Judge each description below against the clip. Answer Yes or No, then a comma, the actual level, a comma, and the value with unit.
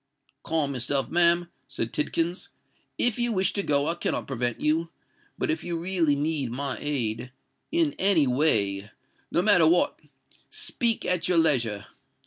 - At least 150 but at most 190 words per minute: No, slow, 135 wpm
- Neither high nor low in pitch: Yes, medium, 155 Hz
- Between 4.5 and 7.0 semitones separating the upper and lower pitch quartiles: Yes, average, 5.0 semitones